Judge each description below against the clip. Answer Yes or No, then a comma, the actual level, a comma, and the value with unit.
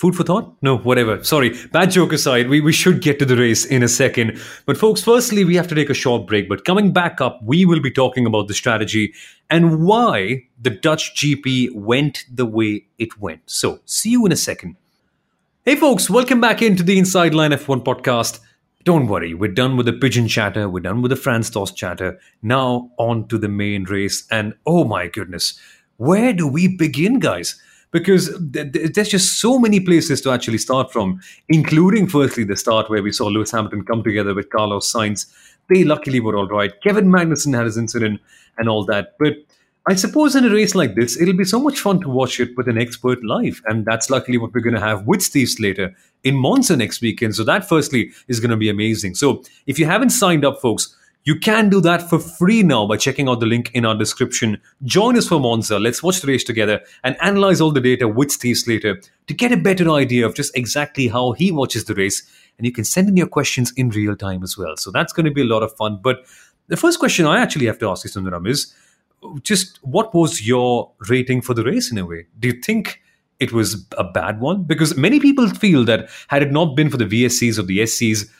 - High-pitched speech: No, low, 130 Hz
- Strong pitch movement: Yes, wide, 7.2 semitones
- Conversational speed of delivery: No, fast, 225 wpm